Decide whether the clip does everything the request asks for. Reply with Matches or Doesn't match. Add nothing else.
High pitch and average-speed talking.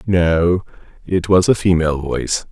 Doesn't match